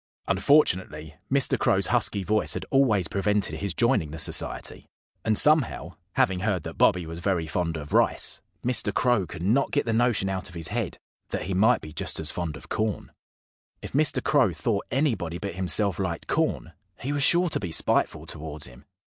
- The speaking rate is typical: Yes, average, 190 wpm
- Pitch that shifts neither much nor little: No, wide, 6.2 semitones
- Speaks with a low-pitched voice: Yes, very low, 95 Hz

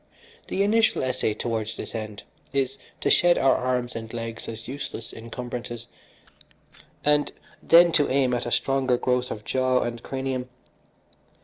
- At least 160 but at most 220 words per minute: No, average, 145 wpm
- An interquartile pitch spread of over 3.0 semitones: No, average, 2.7 semitones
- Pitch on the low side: Yes, low, 125 Hz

